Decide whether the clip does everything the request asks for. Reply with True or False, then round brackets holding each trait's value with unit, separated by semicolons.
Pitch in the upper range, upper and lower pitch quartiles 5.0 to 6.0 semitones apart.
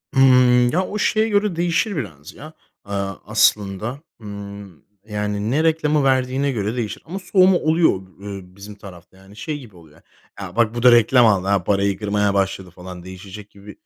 False (105 Hz; 5.6 semitones)